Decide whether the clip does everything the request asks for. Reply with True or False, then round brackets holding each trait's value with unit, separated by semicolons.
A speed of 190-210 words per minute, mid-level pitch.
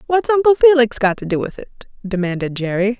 False (200 wpm; 235 Hz)